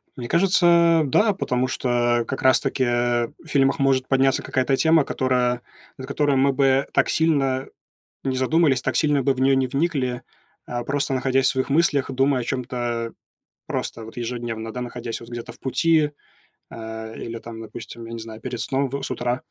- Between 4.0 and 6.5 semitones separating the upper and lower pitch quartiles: No, narrow, 2.5 semitones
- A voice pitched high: No, low, 130 Hz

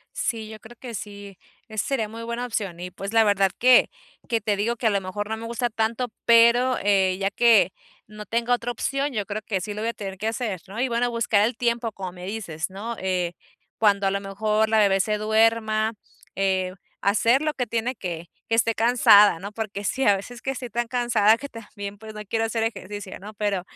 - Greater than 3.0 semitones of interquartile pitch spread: No, average, 2.7 semitones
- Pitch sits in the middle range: No, high, 215 Hz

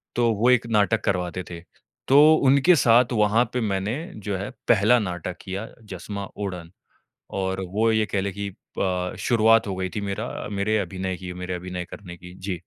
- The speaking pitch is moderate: No, low, 100 Hz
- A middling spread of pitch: Yes, average, 3.2 semitones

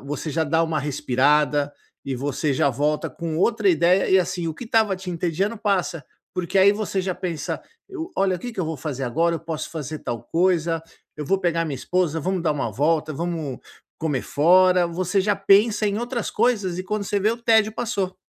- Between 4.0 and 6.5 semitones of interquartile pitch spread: Yes, average, 4.3 semitones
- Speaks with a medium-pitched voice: Yes, medium, 175 Hz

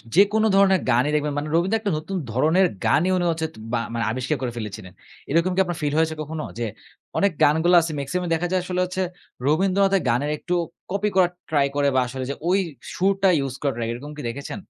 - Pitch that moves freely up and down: No, average, 5.0 semitones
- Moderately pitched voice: Yes, medium, 160 Hz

